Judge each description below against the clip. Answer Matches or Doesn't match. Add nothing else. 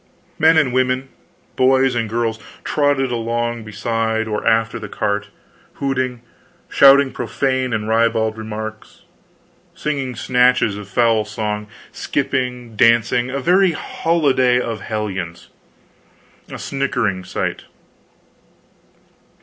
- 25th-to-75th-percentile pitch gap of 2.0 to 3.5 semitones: Matches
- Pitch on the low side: Matches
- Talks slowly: Matches